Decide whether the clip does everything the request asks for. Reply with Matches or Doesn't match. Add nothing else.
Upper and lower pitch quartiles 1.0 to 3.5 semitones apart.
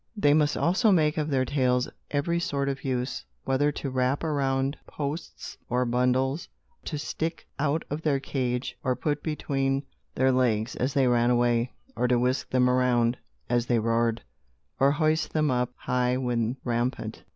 Matches